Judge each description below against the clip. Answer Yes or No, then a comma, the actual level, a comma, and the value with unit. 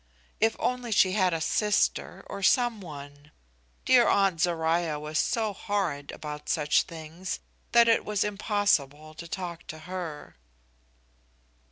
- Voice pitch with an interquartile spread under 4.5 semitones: No, average, 4.9 semitones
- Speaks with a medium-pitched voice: Yes, medium, 175 Hz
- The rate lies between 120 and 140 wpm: Yes, slow, 135 wpm